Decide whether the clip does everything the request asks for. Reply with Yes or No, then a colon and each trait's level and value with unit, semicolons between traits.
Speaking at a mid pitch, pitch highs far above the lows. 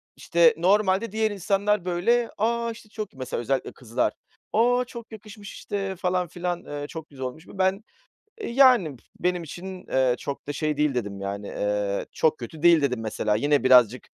Yes: medium, 175 Hz; wide, 7.9 semitones